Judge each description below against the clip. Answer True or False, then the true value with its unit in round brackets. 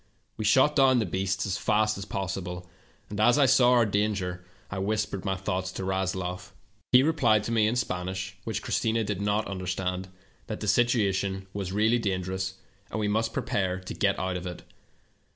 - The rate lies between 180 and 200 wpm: True (185 wpm)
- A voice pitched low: True (100 Hz)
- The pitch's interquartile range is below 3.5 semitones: True (2.8 semitones)